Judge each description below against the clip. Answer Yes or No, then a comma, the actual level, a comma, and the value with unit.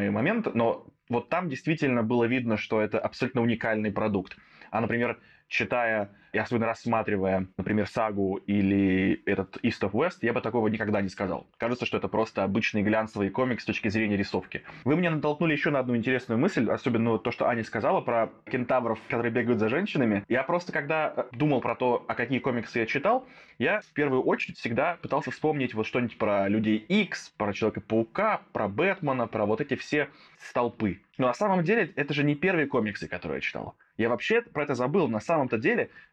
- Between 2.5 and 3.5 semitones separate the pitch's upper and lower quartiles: No, average, 4.7 semitones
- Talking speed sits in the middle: No, fast, 190 wpm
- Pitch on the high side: No, low, 120 Hz